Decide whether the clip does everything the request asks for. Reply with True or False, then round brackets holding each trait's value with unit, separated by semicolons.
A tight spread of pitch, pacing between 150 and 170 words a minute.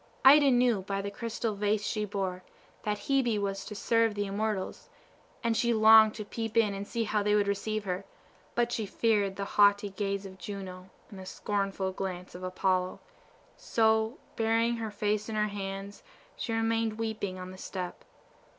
False (2.2 semitones; 180 wpm)